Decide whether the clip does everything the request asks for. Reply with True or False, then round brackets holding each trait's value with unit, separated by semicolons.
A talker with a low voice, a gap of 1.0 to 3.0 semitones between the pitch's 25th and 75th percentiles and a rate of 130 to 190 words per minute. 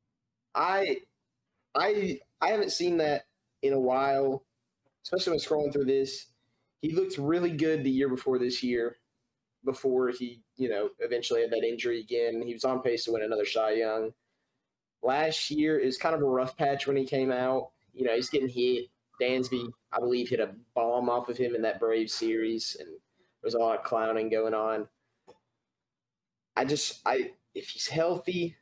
False (130 Hz; 4.6 semitones; 180 wpm)